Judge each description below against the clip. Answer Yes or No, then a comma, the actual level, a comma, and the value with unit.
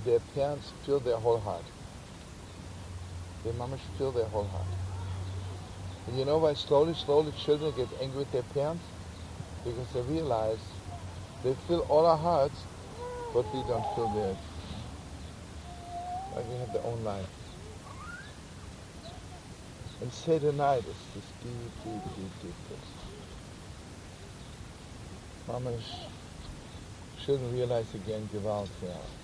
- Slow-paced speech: Yes, slow, 120 wpm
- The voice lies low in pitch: Yes, low, 105 Hz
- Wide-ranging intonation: Yes, wide, 6.5 semitones